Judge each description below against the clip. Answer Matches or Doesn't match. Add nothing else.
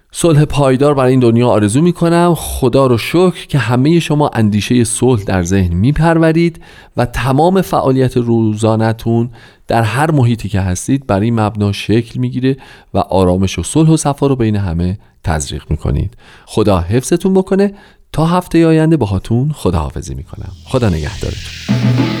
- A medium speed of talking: Doesn't match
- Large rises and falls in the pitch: Matches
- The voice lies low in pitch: Matches